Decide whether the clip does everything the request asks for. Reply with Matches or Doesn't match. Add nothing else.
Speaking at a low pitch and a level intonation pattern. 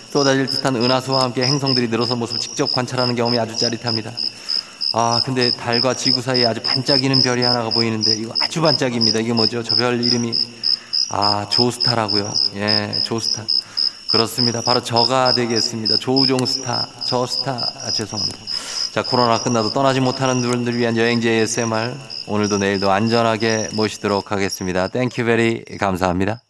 Matches